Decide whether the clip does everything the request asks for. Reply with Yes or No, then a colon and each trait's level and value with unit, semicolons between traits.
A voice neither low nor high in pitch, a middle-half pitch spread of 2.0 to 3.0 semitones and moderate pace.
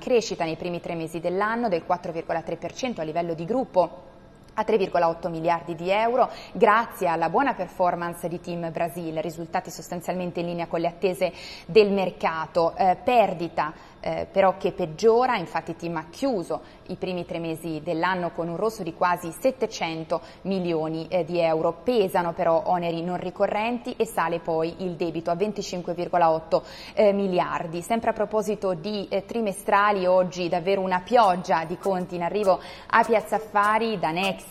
Yes: medium, 180 Hz; average, 2.7 semitones; average, 160 wpm